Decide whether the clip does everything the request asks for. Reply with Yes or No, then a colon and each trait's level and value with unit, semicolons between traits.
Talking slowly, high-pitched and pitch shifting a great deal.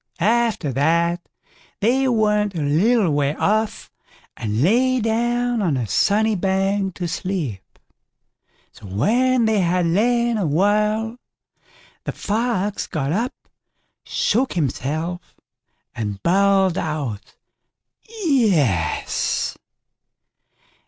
Yes: slow, 100 wpm; high, 195 Hz; wide, 6.2 semitones